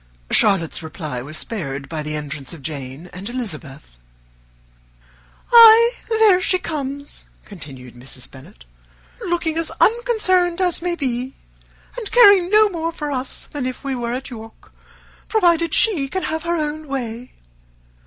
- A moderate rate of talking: Yes, average, 145 wpm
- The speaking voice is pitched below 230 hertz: No, very high, 270 Hz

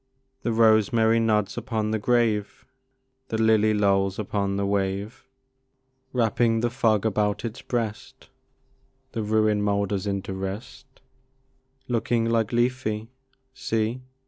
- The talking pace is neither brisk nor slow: No, slow, 115 wpm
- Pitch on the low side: Yes, low, 110 Hz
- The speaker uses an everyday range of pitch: No, narrow, 2.1 semitones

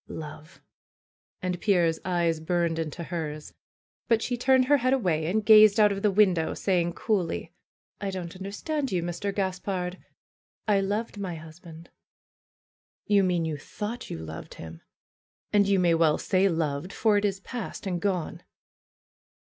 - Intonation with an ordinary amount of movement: Yes, average, 3.8 semitones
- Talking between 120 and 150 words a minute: No, average, 165 wpm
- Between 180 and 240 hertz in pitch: Yes, medium, 185 Hz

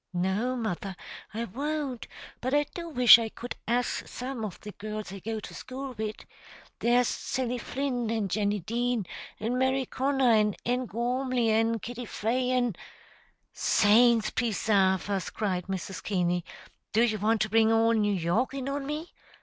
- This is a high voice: Yes, high, 230 Hz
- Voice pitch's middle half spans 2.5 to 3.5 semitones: Yes, average, 3.1 semitones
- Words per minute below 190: Yes, average, 165 wpm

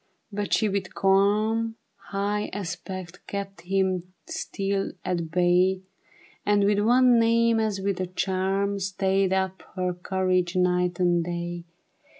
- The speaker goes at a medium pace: No, slow, 130 wpm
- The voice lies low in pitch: No, high, 190 Hz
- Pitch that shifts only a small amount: Yes, narrow, 1.9 semitones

